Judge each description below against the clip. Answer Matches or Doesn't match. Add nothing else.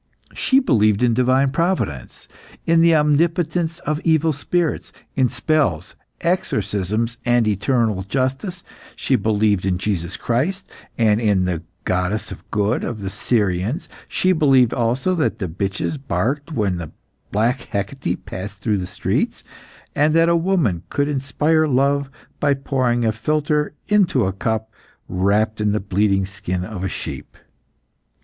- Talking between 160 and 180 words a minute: Doesn't match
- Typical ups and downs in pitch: Doesn't match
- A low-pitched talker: Matches